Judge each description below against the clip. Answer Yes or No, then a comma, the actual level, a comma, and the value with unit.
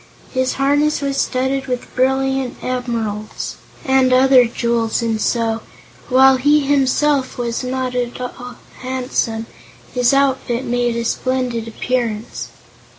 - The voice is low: No, very high, 255 Hz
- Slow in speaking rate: Yes, slow, 120 wpm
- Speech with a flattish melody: Yes, narrow, 2.0 semitones